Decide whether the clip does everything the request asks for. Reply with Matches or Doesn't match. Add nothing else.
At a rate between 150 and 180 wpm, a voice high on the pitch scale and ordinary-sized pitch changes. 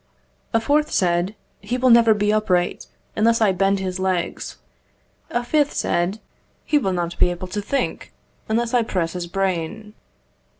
Matches